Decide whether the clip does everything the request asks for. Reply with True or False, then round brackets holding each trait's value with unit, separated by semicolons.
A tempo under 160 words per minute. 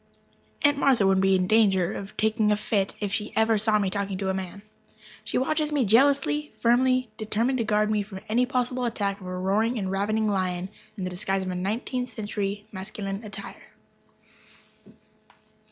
False (175 wpm)